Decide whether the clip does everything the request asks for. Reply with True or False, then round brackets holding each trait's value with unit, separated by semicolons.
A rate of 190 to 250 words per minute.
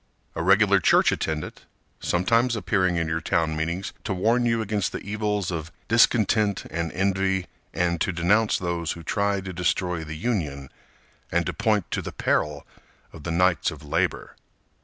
False (165 wpm)